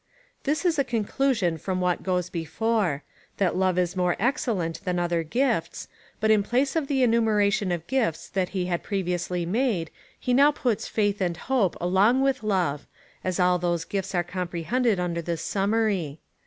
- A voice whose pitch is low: No, high, 190 Hz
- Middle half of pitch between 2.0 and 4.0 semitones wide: No, average, 4.7 semitones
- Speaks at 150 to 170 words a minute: No, average, 180 wpm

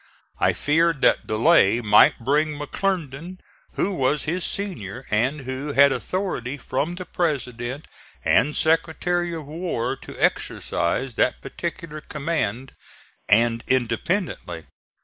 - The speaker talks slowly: Yes, slow, 115 wpm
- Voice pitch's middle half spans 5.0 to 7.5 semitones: Yes, wide, 5.6 semitones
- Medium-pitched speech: Yes, medium, 145 Hz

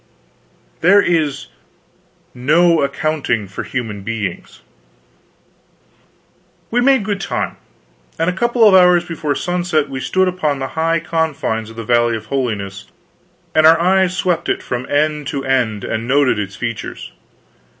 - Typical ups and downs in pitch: No, wide, 6.7 semitones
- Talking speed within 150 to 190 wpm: No, average, 140 wpm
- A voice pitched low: No, medium, 150 Hz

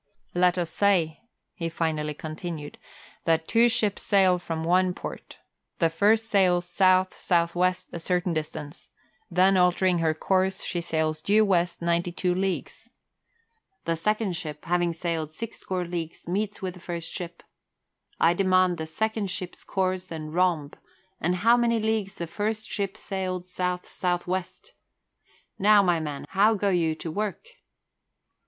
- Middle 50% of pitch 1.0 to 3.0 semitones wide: Yes, narrow, 2.6 semitones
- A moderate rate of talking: Yes, average, 155 wpm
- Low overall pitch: No, medium, 180 Hz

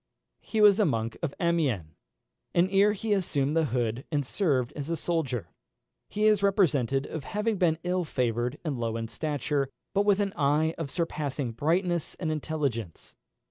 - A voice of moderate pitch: Yes, medium, 155 Hz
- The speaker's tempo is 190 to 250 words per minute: No, average, 170 wpm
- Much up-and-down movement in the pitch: Yes, wide, 5.9 semitones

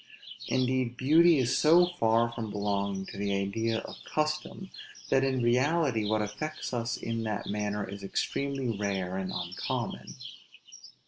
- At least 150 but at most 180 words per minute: No, average, 140 wpm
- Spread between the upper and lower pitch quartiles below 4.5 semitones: No, average, 4.8 semitones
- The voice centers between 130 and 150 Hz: No, low, 115 Hz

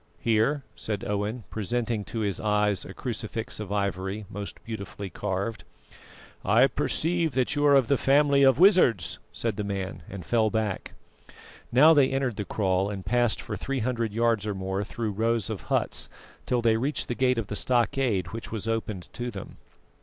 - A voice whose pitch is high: No, low, 110 Hz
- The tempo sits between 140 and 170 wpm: No, average, 180 wpm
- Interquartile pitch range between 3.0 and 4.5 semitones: Yes, average, 3.6 semitones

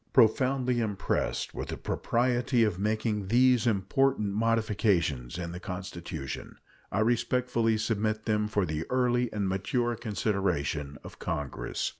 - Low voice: Yes, low, 110 Hz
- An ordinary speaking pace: No, slow, 125 wpm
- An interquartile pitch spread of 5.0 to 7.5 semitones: No, average, 4.2 semitones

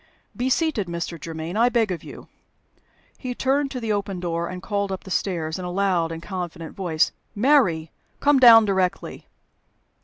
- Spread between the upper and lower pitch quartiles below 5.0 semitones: No, average, 5.3 semitones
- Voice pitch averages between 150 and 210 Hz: Yes, high, 190 Hz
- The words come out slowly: No, average, 175 wpm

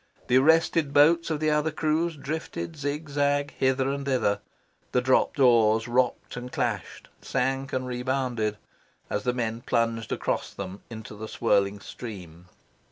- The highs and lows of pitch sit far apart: No, average, 4.0 semitones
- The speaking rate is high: No, average, 145 wpm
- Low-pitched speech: Yes, low, 130 Hz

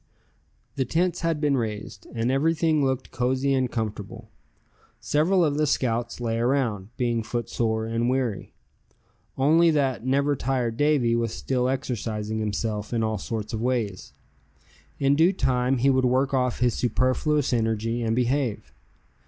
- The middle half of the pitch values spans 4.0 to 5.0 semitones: No, average, 3.4 semitones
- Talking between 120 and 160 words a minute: Yes, average, 145 wpm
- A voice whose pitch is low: Yes, low, 125 Hz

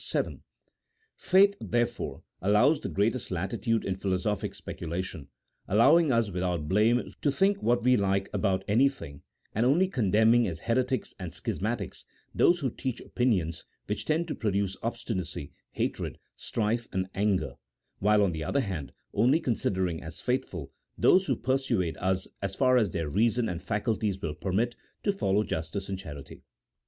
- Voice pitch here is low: Yes, low, 105 Hz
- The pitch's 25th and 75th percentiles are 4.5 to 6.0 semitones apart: Yes, average, 4.9 semitones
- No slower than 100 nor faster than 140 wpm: No, average, 155 wpm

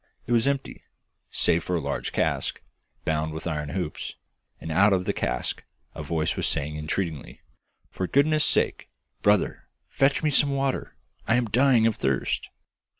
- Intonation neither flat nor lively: No, wide, 9.0 semitones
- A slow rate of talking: No, average, 160 wpm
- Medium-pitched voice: No, very low, 95 Hz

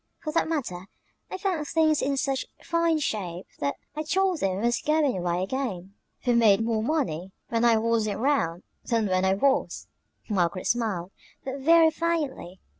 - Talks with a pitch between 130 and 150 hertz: No, high, 235 Hz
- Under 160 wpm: No, average, 170 wpm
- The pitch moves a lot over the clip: Yes, wide, 8.1 semitones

